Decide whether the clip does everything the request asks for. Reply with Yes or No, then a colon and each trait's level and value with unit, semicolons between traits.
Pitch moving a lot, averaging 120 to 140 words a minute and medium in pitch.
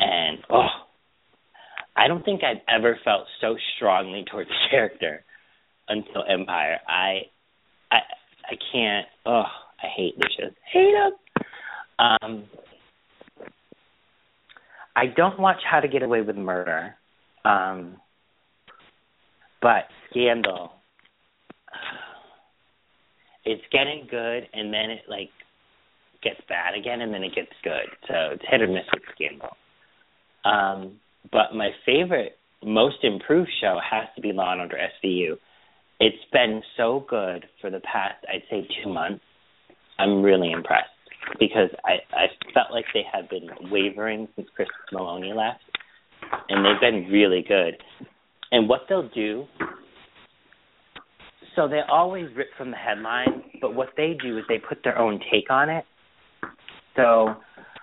No: wide, 6.0 semitones; slow, 135 wpm; low, 115 Hz